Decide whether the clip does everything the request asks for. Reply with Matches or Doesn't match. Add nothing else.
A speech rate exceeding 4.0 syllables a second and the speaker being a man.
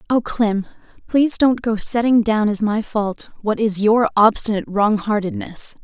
Doesn't match